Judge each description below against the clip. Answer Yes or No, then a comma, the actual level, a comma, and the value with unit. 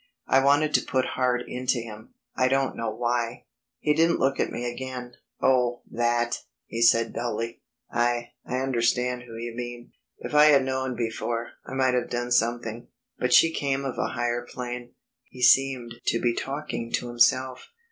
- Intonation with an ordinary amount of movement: No, narrow, 1.8 semitones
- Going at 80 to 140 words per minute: No, average, 175 wpm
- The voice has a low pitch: Yes, low, 125 Hz